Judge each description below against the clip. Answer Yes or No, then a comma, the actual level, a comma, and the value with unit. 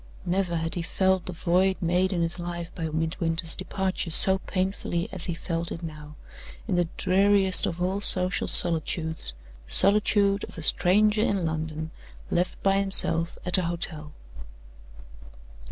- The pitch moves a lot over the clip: No, narrow, 2.5 semitones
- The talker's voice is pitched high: No, medium, 175 Hz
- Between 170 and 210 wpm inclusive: No, average, 155 wpm